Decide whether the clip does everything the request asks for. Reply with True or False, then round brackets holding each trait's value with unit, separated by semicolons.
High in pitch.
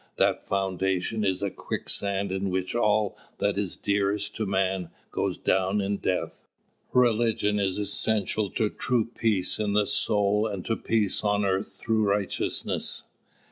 False (100 Hz)